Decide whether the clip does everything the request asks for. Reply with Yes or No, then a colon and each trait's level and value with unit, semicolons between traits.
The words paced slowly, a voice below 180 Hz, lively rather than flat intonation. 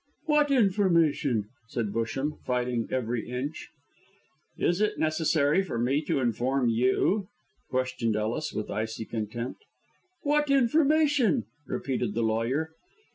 Yes: slow, 115 wpm; low, 135 Hz; wide, 8.5 semitones